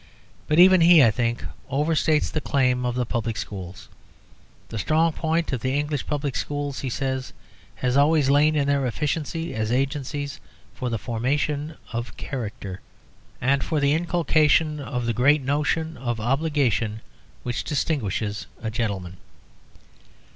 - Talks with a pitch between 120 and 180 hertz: Yes, medium, 140 Hz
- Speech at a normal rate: Yes, average, 145 wpm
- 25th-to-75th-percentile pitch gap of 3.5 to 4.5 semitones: Yes, average, 4.1 semitones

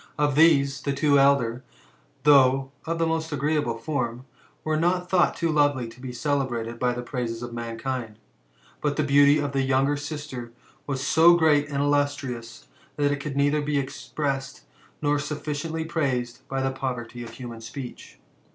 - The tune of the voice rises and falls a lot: No, average, 3.0 semitones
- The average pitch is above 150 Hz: No, medium, 140 Hz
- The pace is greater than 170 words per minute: No, average, 165 wpm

